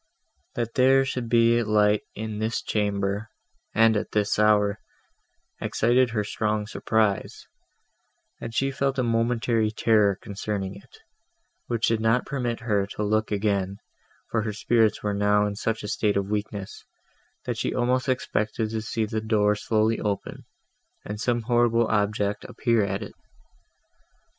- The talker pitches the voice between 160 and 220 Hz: No, low, 110 Hz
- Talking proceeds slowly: No, average, 150 wpm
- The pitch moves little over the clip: Yes, narrow, 1.9 semitones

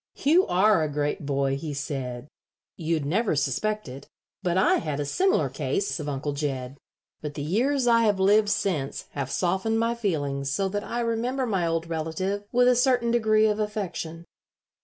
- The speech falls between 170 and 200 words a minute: Yes, average, 180 wpm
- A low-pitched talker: No, medium, 185 Hz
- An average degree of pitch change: No, wide, 7.3 semitones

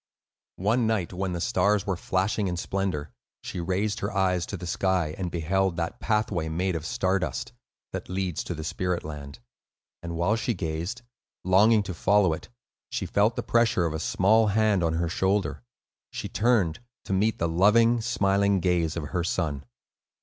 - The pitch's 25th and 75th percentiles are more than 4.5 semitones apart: No, average, 3.5 semitones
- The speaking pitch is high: No, very low, 95 Hz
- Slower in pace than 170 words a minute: No, average, 180 wpm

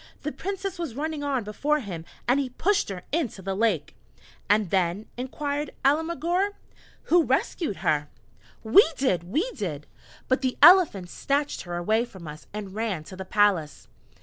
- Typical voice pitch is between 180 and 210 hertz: No, high, 230 Hz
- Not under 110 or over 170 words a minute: Yes, average, 160 wpm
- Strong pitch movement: Yes, wide, 8.2 semitones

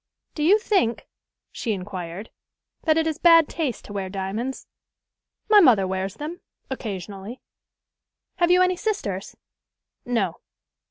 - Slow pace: Yes, slow, 125 wpm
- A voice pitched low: No, high, 240 Hz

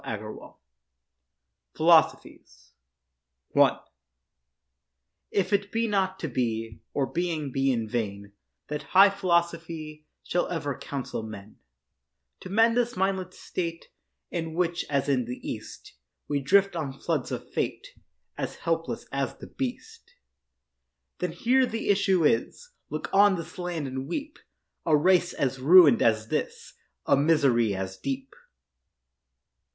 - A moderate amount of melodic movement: No, wide, 5.9 semitones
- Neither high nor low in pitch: Yes, medium, 160 Hz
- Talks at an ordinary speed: No, slow, 125 wpm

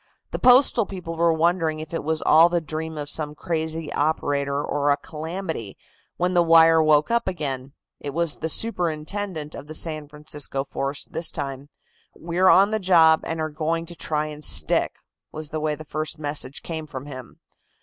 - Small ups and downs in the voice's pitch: Yes, narrow, 2.2 semitones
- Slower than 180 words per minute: No, average, 185 wpm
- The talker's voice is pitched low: No, medium, 155 Hz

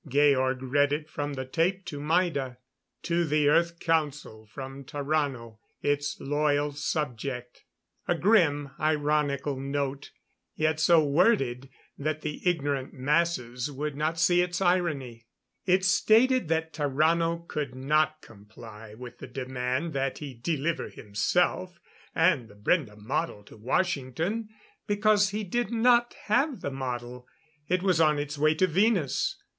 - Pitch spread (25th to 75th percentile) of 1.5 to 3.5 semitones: No, average, 4.3 semitones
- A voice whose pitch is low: No, medium, 150 Hz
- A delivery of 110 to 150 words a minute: Yes, average, 140 wpm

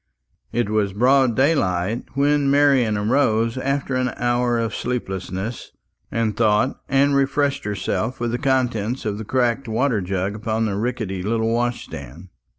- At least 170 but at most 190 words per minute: No, average, 150 wpm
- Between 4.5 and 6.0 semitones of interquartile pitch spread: No, average, 3.7 semitones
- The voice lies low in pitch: Yes, low, 120 Hz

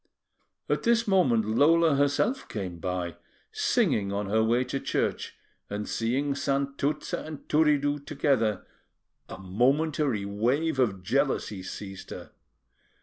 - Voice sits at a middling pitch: No, low, 130 Hz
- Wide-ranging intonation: Yes, wide, 6.0 semitones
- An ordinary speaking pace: No, slow, 120 wpm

